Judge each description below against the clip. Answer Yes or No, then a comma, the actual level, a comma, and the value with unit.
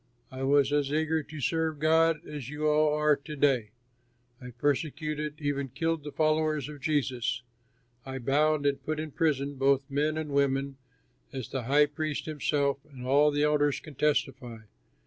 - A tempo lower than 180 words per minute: Yes, average, 170 wpm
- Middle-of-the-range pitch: Yes, medium, 145 Hz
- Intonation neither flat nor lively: No, narrow, 1.9 semitones